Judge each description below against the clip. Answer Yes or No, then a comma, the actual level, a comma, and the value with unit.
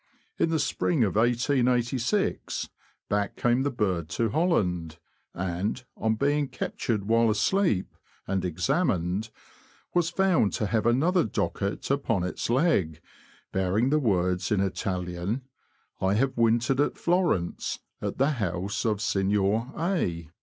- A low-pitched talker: Yes, low, 110 Hz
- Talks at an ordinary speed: No, slow, 130 wpm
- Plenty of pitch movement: Yes, wide, 6.3 semitones